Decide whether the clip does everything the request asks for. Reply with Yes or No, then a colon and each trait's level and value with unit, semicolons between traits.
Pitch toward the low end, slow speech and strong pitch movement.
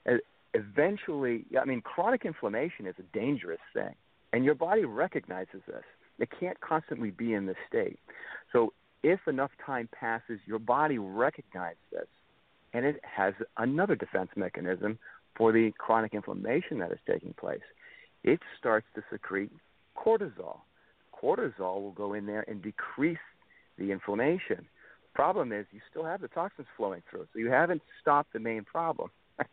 No: low, 115 Hz; average, 150 wpm; wide, 6.6 semitones